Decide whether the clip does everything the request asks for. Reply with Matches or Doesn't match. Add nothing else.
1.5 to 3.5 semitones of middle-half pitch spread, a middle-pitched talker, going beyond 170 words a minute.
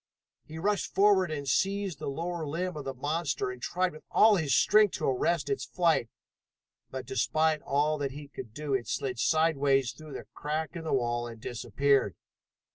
Doesn't match